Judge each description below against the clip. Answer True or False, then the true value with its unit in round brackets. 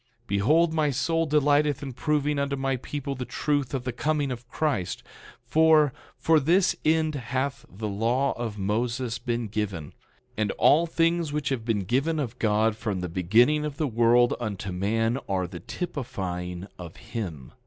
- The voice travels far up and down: True (5.9 semitones)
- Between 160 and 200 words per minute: True (170 wpm)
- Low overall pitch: True (125 Hz)